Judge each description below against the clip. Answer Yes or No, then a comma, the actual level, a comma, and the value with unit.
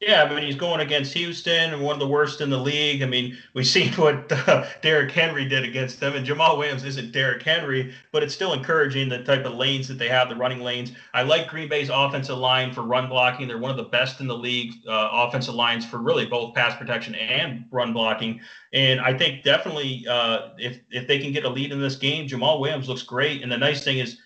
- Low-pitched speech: Yes, low, 130 Hz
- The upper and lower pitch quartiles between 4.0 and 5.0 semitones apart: No, average, 2.8 semitones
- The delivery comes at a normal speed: No, fast, 240 wpm